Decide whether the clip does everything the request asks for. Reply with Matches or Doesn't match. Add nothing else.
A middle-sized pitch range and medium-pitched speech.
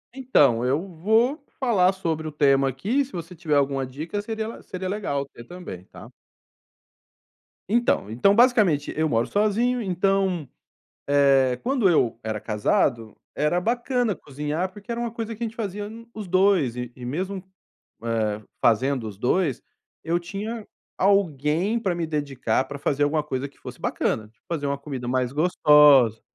Doesn't match